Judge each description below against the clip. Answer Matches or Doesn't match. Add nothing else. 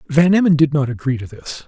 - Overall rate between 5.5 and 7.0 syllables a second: Matches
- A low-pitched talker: Doesn't match